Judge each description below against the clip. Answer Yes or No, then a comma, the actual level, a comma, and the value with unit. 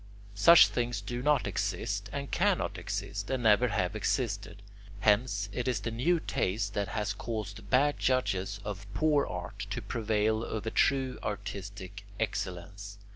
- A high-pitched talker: No, low, 105 Hz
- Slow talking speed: No, average, 145 wpm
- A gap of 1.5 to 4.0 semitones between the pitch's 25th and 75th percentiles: Yes, average, 3.4 semitones